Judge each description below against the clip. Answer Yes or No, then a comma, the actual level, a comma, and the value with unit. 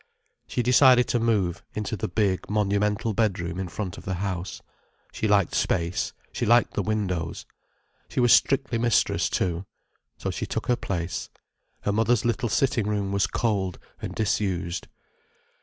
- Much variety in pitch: No, average, 3.7 semitones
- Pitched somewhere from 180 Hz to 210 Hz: No, low, 105 Hz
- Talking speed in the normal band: Yes, average, 155 wpm